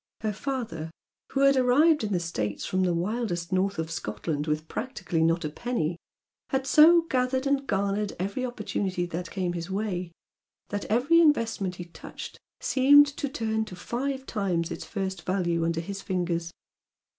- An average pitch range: No, wide, 6.6 semitones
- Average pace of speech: Yes, average, 170 wpm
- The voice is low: No, high, 195 Hz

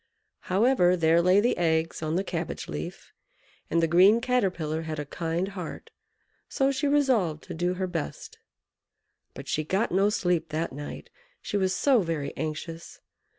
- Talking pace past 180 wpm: No, average, 160 wpm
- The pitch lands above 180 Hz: No, medium, 175 Hz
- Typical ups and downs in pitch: Yes, average, 3.7 semitones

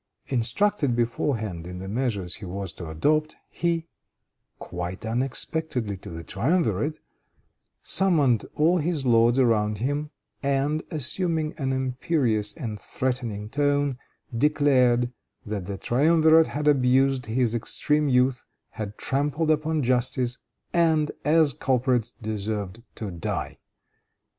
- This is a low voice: Yes, low, 130 Hz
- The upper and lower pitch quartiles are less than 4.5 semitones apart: No, wide, 5.4 semitones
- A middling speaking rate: No, slow, 115 wpm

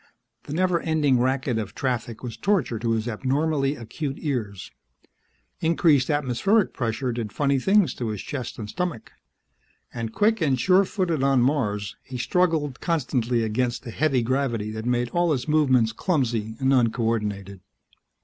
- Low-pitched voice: Yes, low, 130 Hz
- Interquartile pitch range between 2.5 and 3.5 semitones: No, average, 4.9 semitones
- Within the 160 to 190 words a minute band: No, average, 150 wpm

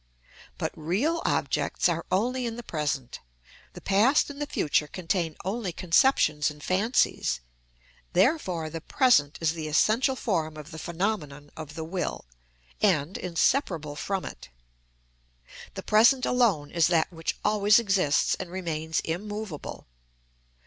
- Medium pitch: Yes, medium, 180 Hz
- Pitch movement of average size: No, wide, 5.7 semitones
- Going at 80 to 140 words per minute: Yes, slow, 135 wpm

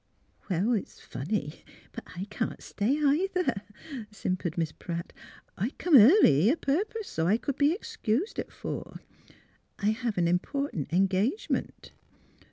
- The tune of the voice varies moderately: No, wide, 8.2 semitones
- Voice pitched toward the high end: Yes, high, 215 Hz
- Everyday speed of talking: Yes, average, 145 wpm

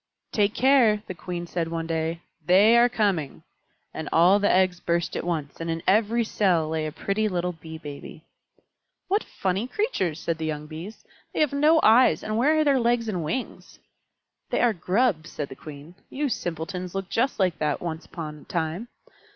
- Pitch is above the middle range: No, medium, 180 Hz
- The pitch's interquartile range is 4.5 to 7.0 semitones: Yes, wide, 5.6 semitones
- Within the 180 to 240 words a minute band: Yes, average, 190 wpm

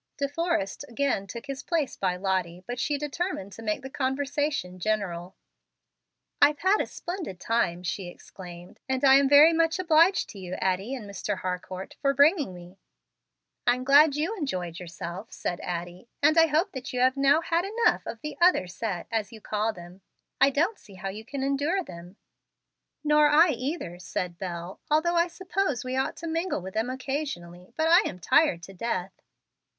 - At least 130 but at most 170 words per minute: No, average, 180 wpm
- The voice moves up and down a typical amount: No, wide, 8.5 semitones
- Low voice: No, very high, 255 Hz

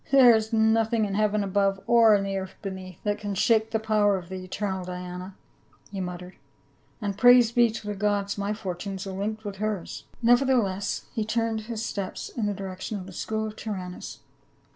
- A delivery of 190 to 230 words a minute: Yes, average, 200 wpm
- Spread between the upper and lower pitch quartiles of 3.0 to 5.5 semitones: No, narrow, 2.5 semitones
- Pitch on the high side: Yes, high, 205 Hz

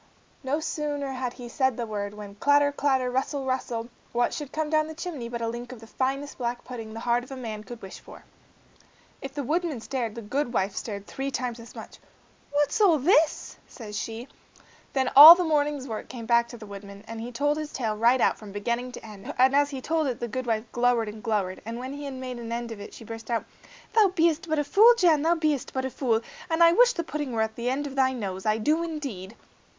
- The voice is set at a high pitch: Yes, very high, 255 Hz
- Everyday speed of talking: No, fast, 230 wpm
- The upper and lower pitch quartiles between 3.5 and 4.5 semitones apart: Yes, average, 4.2 semitones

